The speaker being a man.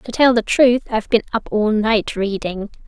No: female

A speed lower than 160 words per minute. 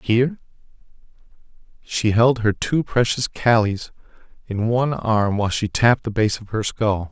Yes: average, 150 wpm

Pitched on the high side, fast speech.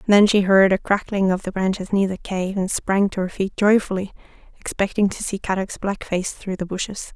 Yes: high, 195 Hz; fast, 220 wpm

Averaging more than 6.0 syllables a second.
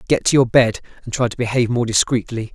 Yes: 6.6 syllables/s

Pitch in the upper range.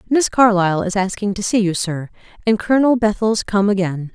Yes: high, 205 Hz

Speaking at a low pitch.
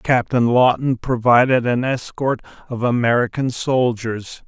Yes: low, 125 Hz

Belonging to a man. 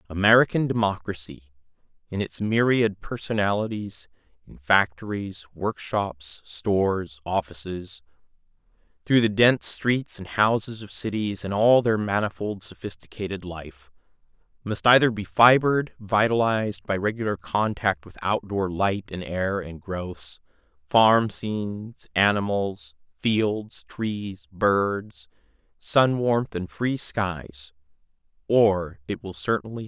Yes: male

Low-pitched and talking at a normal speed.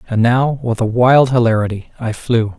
Yes: low, 120 Hz; average, 185 wpm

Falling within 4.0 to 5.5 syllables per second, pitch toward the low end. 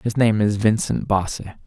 Yes: 5.0 syllables/s; low, 105 Hz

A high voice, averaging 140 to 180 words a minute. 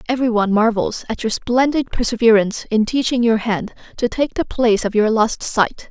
No: high, 230 Hz; average, 195 wpm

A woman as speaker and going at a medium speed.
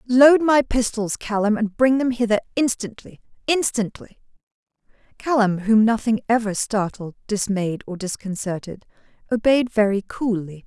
No: female; slow, 120 wpm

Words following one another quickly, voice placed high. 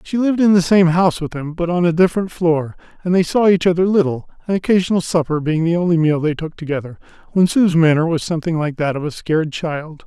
No: fast, 240 wpm; medium, 170 Hz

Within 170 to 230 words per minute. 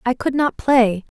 Yes: average, 200 wpm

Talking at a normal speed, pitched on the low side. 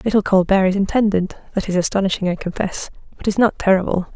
No: average, 190 wpm; high, 195 Hz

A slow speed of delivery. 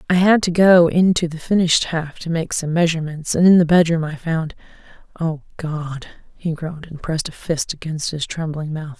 No: average, 195 wpm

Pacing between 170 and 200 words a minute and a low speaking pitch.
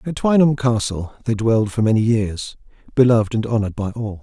Yes: average, 185 wpm; low, 115 Hz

